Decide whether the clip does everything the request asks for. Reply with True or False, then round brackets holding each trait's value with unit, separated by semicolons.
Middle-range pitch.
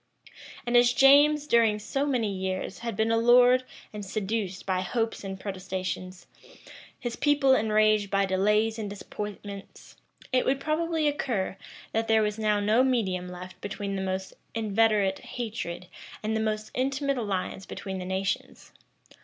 False (215 Hz)